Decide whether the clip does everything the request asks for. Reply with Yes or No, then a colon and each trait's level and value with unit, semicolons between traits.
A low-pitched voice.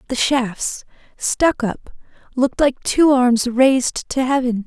No: very high, 255 Hz